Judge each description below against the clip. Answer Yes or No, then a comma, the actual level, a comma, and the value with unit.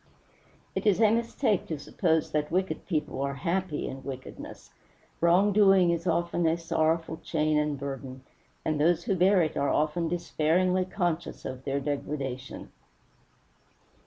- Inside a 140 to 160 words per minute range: Yes, average, 145 wpm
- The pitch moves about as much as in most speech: Yes, average, 3.7 semitones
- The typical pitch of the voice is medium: Yes, medium, 165 Hz